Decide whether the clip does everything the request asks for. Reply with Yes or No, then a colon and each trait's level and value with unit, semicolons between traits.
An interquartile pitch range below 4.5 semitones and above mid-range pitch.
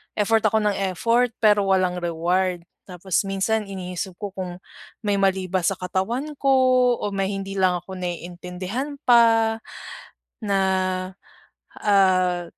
Yes: narrow, 2.6 semitones; high, 195 Hz